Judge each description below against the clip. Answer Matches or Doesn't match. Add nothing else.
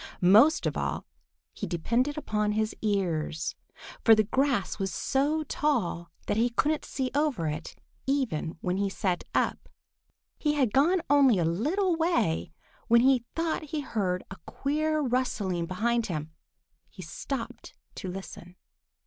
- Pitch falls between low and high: Doesn't match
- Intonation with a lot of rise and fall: Matches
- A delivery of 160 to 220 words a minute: Doesn't match